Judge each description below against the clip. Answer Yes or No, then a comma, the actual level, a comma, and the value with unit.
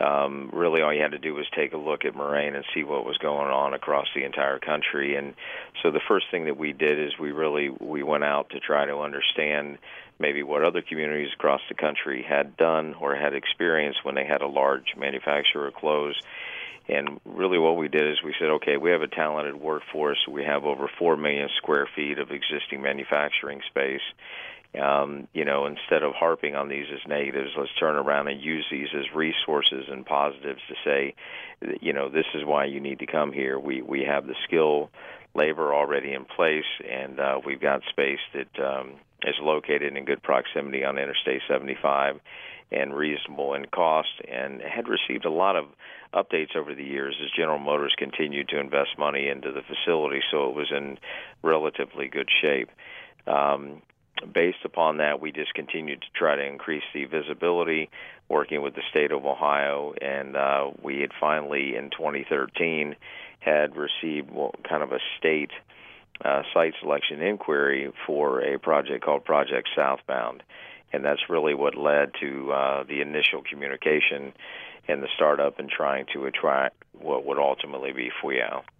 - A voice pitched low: Yes, very low, 70 Hz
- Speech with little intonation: Yes, narrow, 1.2 semitones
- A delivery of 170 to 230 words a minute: Yes, average, 180 wpm